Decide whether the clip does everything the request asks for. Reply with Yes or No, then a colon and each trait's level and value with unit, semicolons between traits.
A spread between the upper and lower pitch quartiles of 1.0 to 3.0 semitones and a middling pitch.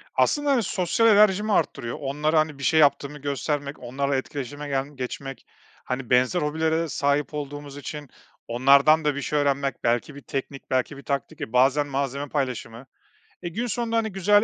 Yes: average, 2.7 semitones; medium, 145 Hz